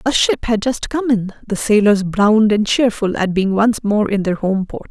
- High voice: Yes, high, 215 Hz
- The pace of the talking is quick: Yes, fast, 230 wpm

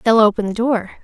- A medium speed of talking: No, fast, 235 wpm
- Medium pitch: No, high, 220 Hz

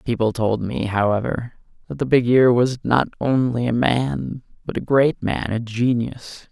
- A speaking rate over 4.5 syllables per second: No, 4.4 syllables/s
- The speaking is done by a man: Yes, male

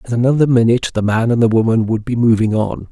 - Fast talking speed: Yes, fast, 245 wpm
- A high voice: No, low, 115 Hz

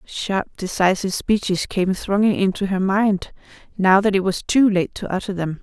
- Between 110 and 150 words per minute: No, average, 180 wpm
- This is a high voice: Yes, high, 195 Hz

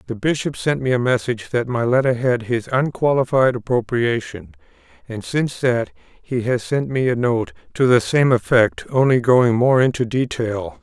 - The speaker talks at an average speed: Yes, average, 170 wpm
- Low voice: Yes, low, 125 Hz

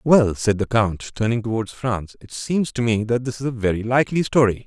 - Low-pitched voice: Yes, low, 115 Hz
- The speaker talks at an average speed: No, fast, 230 wpm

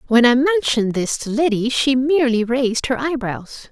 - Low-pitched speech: No, very high, 255 Hz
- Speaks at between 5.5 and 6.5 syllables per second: No, 5.1 syllables/s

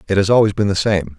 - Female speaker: No, male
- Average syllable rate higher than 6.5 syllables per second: Yes, 6.9 syllables/s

